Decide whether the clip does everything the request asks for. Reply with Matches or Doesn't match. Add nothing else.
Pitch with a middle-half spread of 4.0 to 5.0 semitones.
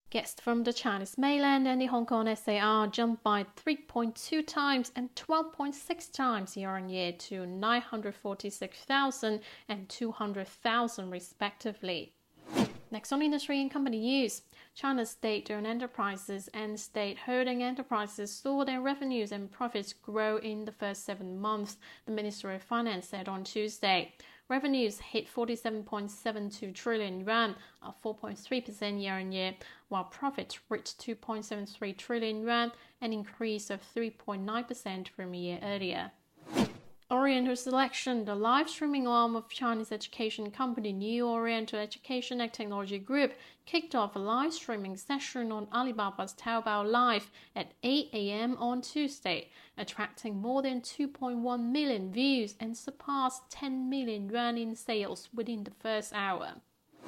Doesn't match